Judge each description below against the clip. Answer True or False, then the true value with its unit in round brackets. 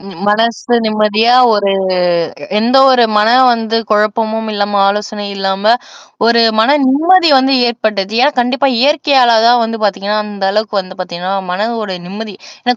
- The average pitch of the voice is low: False (220 Hz)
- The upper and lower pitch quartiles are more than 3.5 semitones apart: False (2.9 semitones)